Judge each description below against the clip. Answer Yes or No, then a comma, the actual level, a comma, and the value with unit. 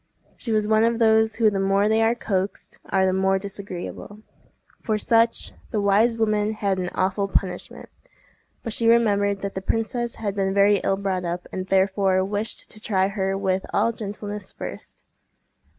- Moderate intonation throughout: No, narrow, 2.2 semitones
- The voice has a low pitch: No, high, 200 Hz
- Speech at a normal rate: Yes, average, 175 wpm